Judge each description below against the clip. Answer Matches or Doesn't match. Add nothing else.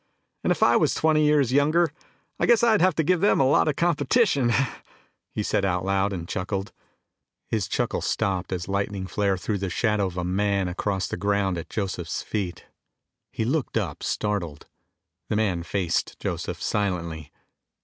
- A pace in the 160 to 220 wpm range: Matches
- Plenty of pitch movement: Matches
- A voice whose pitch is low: Matches